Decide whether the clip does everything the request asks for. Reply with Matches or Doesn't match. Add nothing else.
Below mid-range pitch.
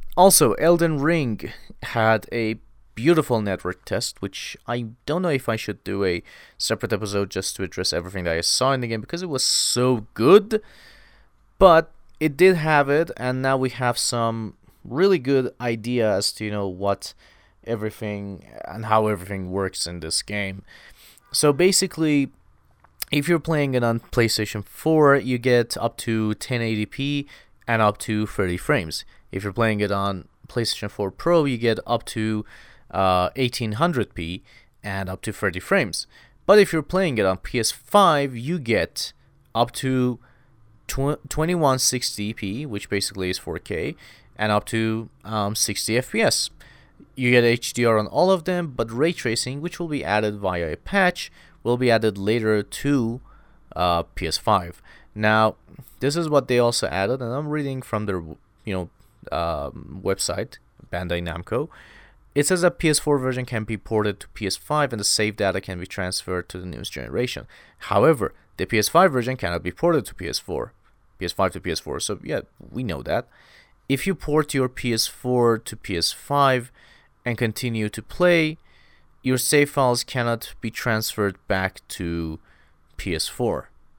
Matches